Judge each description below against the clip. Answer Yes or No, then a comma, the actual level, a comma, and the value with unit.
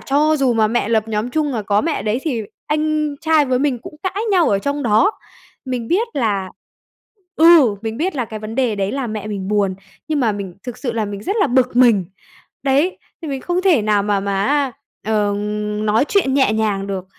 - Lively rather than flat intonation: Yes, wide, 5.8 semitones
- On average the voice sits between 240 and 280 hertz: Yes, high, 245 Hz